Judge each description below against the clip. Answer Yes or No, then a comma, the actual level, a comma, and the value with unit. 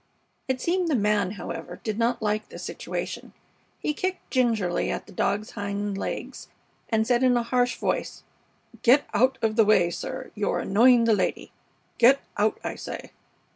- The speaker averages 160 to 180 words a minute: Yes, average, 170 wpm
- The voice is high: Yes, high, 225 Hz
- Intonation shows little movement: No, average, 3.6 semitones